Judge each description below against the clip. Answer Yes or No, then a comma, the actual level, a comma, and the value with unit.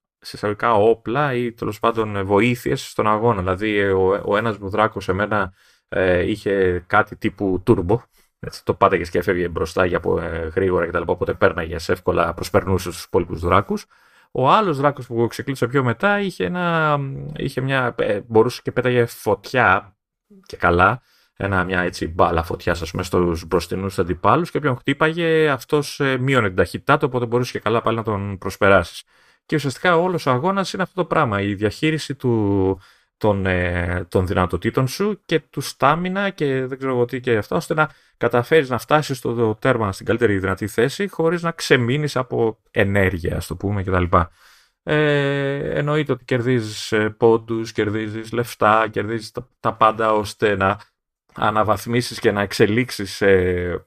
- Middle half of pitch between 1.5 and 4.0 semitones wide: No, wide, 5.6 semitones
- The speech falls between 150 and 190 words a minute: Yes, average, 155 wpm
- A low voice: Yes, low, 115 Hz